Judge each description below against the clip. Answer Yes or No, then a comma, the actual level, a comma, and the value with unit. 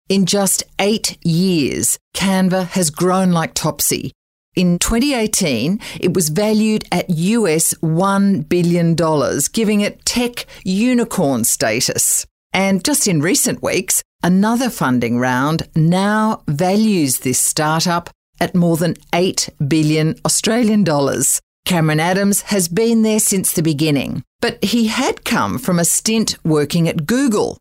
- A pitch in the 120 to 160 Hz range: No, medium, 185 Hz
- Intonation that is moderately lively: Yes, average, 4.4 semitones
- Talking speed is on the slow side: Yes, slow, 130 wpm